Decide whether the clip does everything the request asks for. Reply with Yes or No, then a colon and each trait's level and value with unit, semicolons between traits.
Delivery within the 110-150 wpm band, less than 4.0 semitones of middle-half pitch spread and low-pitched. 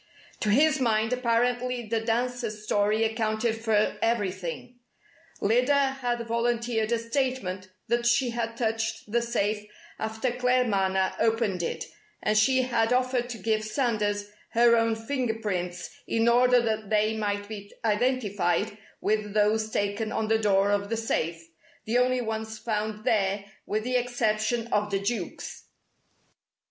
No: average, 140 wpm; narrow, 2.4 semitones; high, 225 Hz